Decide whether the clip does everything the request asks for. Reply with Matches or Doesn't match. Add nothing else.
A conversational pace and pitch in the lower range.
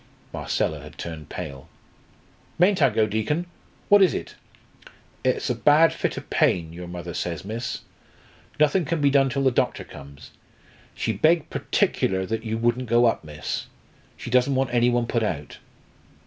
Matches